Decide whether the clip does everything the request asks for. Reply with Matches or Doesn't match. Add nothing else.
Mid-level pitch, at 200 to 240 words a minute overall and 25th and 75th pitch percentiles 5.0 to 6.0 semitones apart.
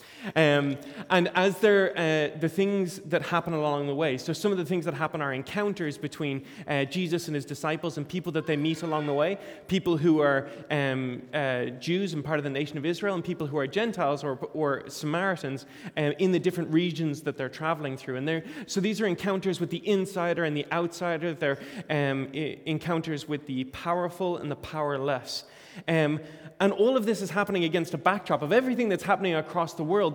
Doesn't match